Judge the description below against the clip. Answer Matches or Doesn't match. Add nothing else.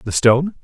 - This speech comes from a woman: Doesn't match